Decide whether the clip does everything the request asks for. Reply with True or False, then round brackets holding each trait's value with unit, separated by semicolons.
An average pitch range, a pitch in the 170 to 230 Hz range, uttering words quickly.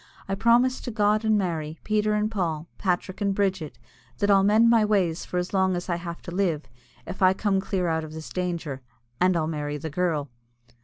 True (3.9 semitones; 185 Hz; 210 wpm)